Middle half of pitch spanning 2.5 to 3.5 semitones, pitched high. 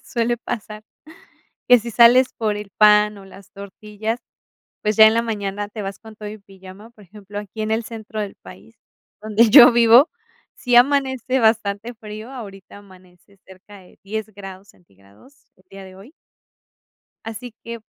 Yes: average, 2.8 semitones; high, 210 Hz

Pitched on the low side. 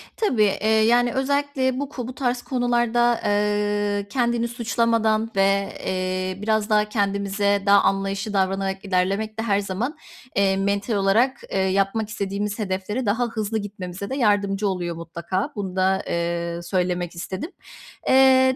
No: high, 205 Hz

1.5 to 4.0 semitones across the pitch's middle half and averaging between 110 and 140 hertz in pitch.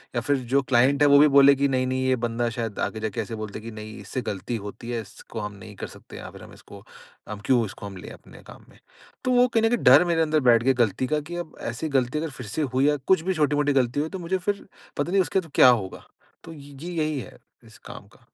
No: average, 4.9 semitones; low, 135 Hz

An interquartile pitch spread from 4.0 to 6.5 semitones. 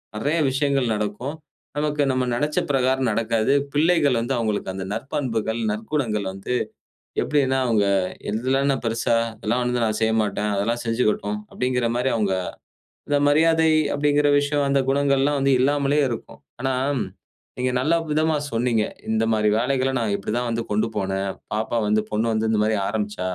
Yes: average, 4.3 semitones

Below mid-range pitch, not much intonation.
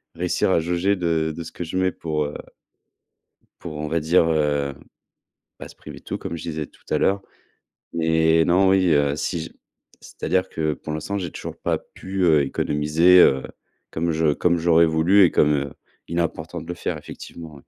Yes: very low, 80 Hz; narrow, 2.2 semitones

